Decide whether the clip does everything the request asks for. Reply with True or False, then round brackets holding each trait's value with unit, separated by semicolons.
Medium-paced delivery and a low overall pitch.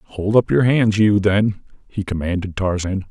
True (175 wpm; 100 Hz)